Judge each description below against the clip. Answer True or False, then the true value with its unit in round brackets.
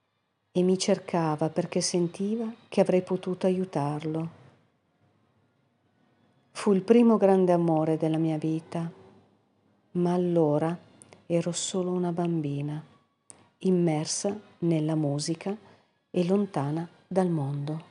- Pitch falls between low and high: True (170 Hz)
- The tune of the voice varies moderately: True (3.4 semitones)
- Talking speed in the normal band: False (100 wpm)